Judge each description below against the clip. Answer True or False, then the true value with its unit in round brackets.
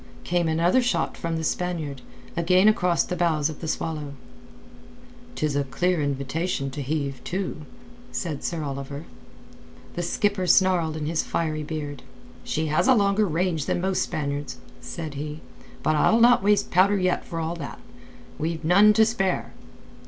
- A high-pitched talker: False (165 Hz)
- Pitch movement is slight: False (3.4 semitones)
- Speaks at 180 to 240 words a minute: False (160 wpm)